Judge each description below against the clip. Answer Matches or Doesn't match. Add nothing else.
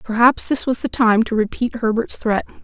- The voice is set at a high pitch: Matches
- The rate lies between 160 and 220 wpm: Matches